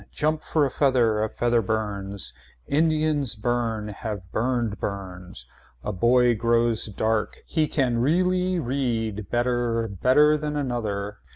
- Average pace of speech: No, slow, 125 wpm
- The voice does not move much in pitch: No, average, 4.6 semitones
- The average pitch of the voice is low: Yes, low, 120 Hz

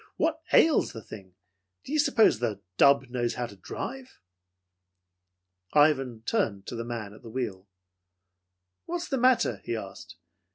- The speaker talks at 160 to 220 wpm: No, average, 150 wpm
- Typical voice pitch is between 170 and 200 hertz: No, low, 120 Hz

